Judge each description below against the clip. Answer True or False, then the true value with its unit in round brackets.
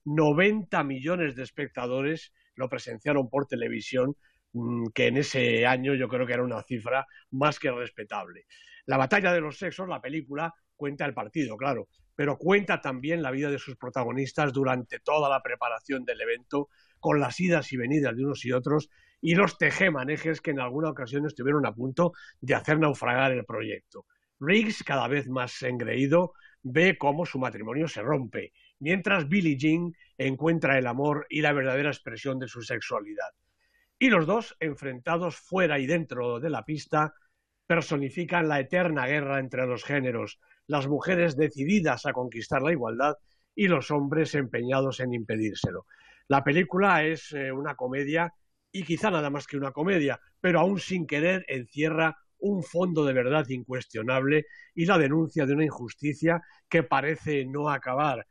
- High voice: False (145 Hz)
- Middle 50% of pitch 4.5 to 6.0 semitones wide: False (4.1 semitones)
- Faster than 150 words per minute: True (160 wpm)